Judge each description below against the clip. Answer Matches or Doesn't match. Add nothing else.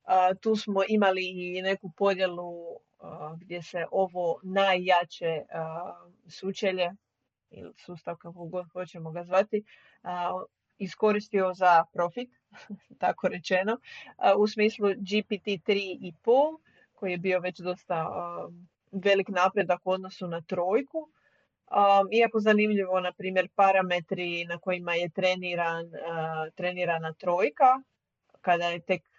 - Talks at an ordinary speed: Matches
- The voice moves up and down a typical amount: Doesn't match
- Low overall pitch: Doesn't match